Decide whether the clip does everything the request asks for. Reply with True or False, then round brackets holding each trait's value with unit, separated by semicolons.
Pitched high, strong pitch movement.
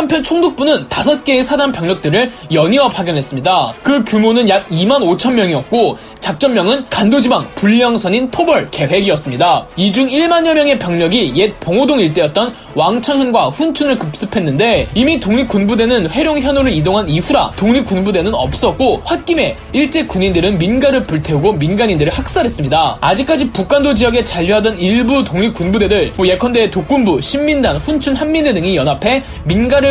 True (240 Hz; 6.7 semitones)